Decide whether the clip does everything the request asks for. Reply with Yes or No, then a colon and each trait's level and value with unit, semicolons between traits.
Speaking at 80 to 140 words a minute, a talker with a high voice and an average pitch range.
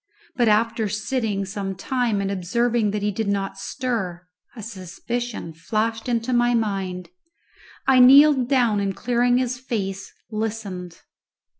Yes: slow, 135 wpm; high, 220 Hz; average, 3.7 semitones